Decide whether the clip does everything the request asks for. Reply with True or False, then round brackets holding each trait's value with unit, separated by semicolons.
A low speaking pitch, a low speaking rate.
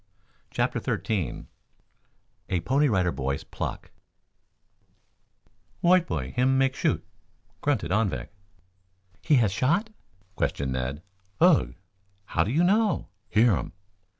True (110 Hz; 110 wpm)